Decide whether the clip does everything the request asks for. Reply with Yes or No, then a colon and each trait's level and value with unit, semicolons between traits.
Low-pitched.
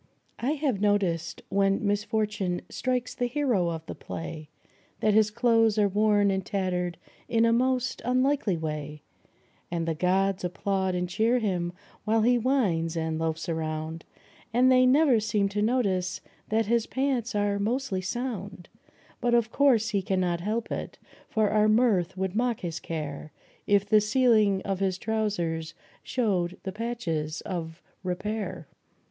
No: high, 205 Hz